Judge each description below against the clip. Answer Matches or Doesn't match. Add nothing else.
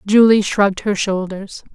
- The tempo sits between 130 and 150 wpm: Matches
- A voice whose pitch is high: Matches